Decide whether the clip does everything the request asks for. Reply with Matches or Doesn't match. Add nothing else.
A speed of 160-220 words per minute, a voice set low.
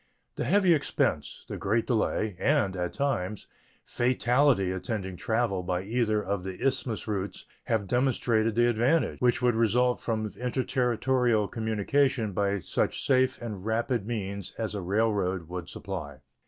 Doesn't match